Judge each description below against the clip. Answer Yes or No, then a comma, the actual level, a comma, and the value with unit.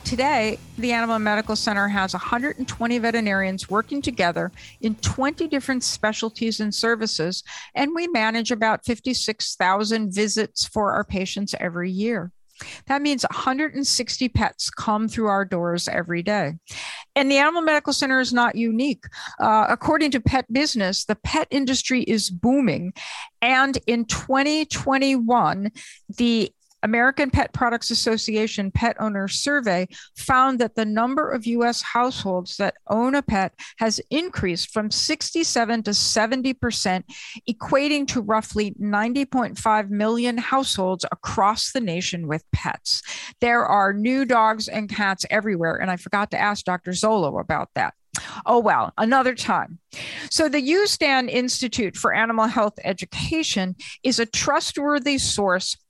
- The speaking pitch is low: No, high, 230 Hz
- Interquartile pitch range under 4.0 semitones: No, average, 4.4 semitones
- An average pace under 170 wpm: Yes, slow, 135 wpm